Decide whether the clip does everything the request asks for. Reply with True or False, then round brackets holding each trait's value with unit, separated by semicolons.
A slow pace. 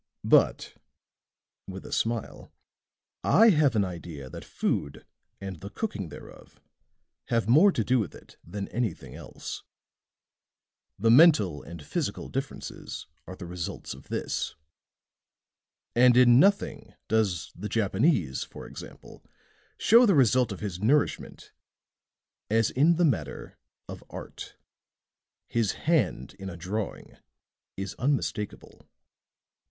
True (120 wpm)